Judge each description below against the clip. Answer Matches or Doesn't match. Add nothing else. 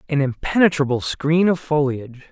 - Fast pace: Doesn't match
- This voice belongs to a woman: Doesn't match